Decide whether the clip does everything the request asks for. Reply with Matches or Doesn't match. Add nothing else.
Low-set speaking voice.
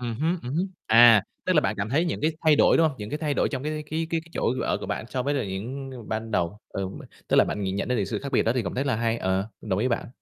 Matches